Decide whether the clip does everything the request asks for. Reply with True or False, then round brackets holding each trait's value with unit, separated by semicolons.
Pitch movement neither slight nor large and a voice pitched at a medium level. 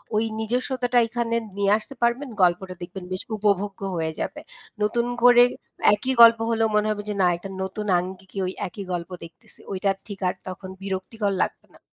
False (3.7 semitones; 205 Hz)